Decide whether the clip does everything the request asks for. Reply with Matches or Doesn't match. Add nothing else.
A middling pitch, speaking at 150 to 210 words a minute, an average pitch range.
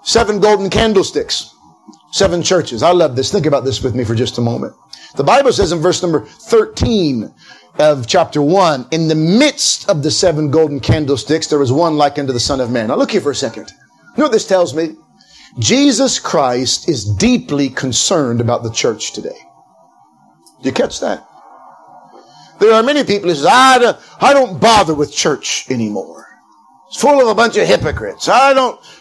Doesn't match